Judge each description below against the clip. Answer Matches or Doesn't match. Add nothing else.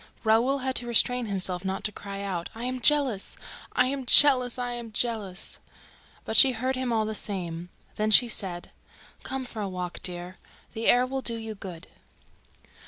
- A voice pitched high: Matches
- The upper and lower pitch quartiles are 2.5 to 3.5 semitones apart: Doesn't match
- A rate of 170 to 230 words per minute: Matches